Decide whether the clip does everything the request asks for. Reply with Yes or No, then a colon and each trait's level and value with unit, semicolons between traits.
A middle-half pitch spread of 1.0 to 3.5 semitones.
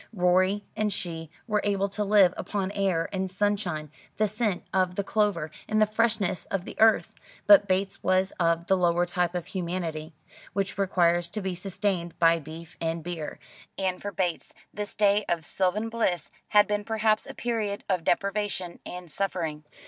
Yes: average, 3.1 semitones